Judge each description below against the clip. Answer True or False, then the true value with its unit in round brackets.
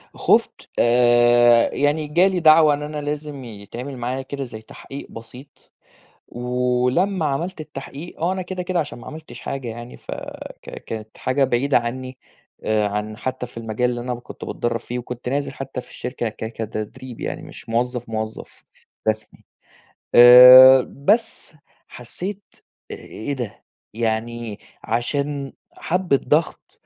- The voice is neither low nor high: False (125 Hz)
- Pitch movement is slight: False (3.7 semitones)